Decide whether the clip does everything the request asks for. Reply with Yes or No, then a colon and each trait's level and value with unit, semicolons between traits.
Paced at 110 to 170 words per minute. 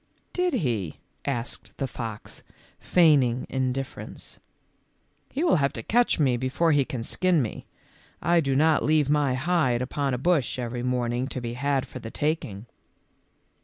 Yes: average, 165 wpm